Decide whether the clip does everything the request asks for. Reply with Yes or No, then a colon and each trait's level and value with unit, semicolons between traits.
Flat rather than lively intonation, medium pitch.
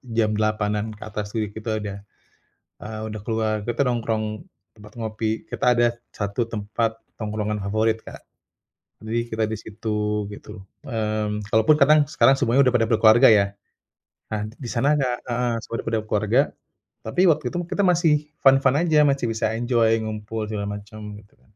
No: narrow, 2.2 semitones; low, 110 Hz